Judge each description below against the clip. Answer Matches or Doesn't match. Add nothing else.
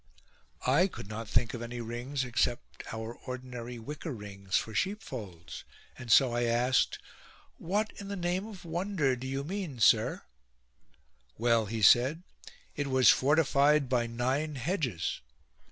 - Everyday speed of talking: Matches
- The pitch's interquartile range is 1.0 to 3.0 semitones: Doesn't match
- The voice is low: Matches